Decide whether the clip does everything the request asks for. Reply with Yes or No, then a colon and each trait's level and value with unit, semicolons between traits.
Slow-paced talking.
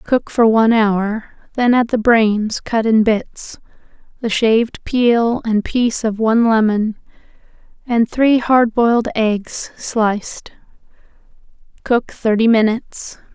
Yes: slow, 125 wpm